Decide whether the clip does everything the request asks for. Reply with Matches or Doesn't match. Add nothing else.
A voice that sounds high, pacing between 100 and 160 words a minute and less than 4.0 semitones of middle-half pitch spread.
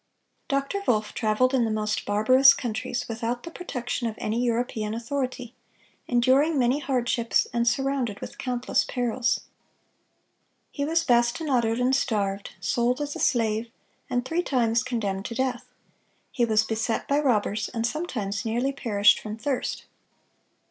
Matches